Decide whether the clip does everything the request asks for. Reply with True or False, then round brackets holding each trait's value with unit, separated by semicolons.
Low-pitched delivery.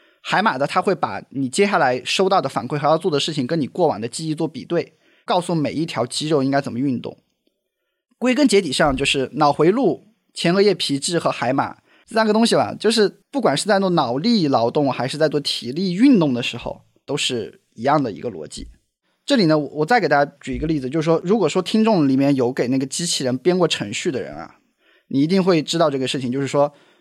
False (160 Hz)